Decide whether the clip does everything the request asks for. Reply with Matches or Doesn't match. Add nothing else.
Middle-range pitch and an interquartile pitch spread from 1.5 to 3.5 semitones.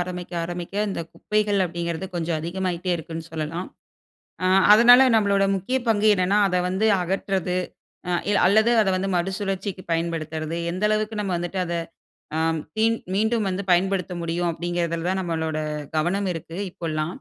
Matches